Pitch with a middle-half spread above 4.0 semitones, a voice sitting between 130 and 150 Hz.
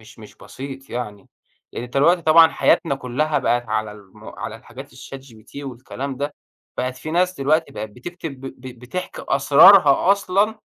Yes: average, 4.7 semitones; low, 135 Hz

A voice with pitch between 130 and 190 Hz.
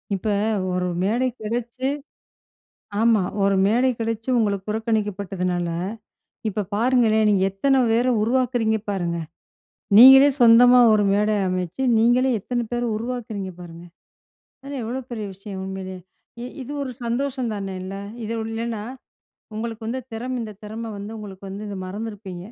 No: high, 220 Hz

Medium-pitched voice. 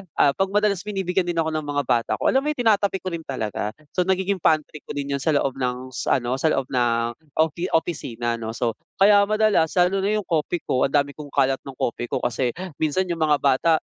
Yes: medium, 155 Hz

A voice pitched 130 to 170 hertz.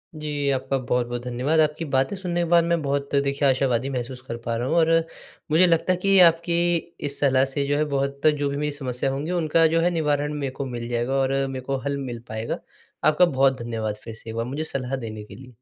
Yes: medium, 140 Hz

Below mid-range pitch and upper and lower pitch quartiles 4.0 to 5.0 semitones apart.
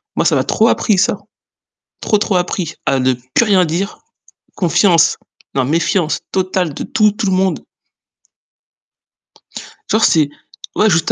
No: medium, 180 Hz; average, 4.3 semitones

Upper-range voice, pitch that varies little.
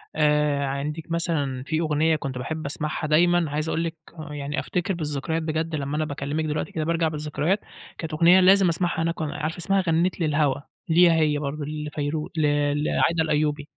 No: medium, 155 Hz; narrow, 1.9 semitones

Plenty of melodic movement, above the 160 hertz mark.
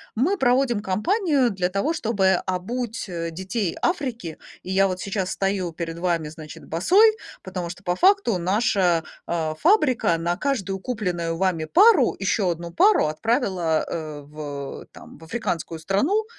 Yes: wide, 6.4 semitones; high, 190 Hz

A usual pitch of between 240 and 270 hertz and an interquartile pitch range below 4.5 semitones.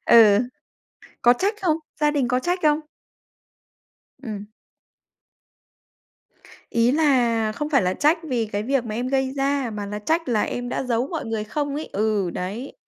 No: high, 245 Hz; average, 5.1 semitones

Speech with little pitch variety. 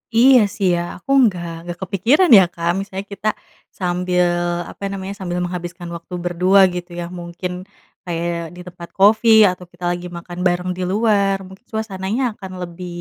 Yes: narrow, 2.1 semitones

